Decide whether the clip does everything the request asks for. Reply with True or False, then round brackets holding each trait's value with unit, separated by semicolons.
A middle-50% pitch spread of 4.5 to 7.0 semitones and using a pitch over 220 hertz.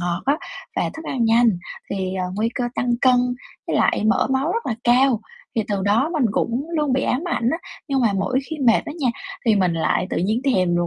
True (5.1 semitones; 240 Hz)